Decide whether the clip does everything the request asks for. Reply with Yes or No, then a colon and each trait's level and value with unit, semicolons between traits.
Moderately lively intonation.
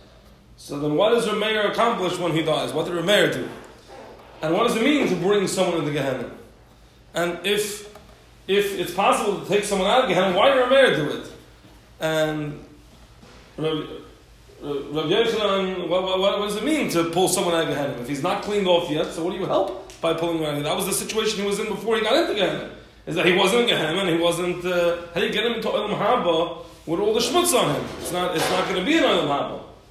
Yes: average, 4.1 semitones